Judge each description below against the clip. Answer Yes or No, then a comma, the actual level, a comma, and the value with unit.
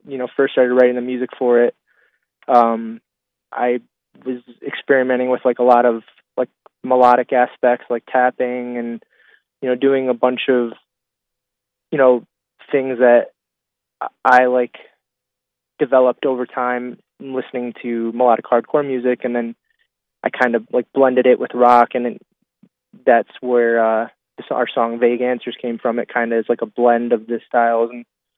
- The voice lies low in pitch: Yes, low, 125 Hz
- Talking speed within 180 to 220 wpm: No, average, 160 wpm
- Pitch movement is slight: Yes, narrow, 1.0 semitones